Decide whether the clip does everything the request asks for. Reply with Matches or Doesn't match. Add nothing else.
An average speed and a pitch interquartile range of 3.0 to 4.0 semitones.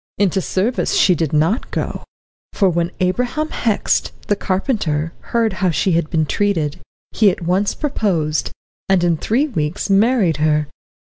Doesn't match